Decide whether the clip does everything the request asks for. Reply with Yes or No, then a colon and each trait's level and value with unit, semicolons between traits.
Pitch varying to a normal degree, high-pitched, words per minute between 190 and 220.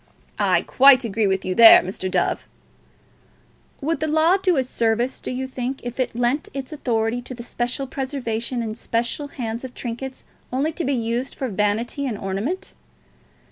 No: average, 3.1 semitones; high, 245 Hz; average, 175 wpm